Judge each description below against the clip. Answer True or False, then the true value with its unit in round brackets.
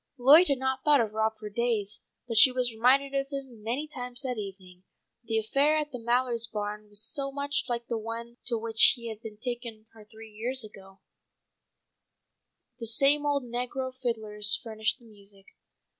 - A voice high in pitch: True (235 Hz)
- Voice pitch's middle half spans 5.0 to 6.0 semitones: False (3.4 semitones)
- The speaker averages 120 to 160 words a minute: False (175 wpm)